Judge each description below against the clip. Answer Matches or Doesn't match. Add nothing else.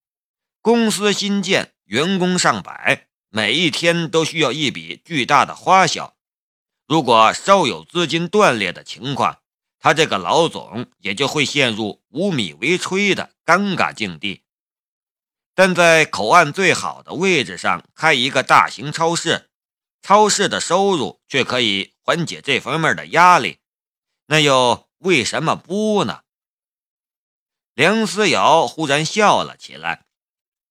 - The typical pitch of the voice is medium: Matches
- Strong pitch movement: Doesn't match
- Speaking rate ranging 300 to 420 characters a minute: Doesn't match